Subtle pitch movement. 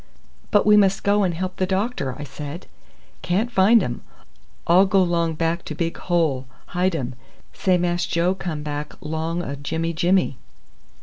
No: average, 3.1 semitones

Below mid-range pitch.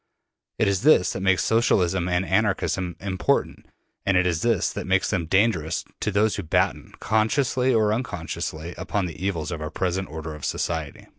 Yes: very low, 95 Hz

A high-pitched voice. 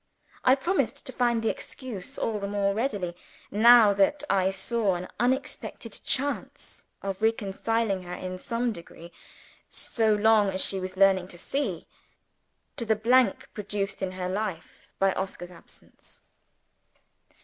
Yes: high, 205 Hz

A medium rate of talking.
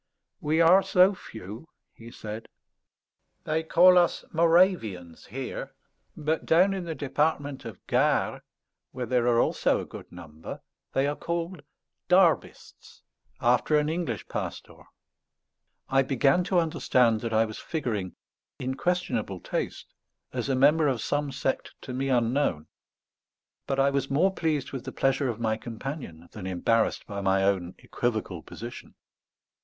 Yes: average, 145 wpm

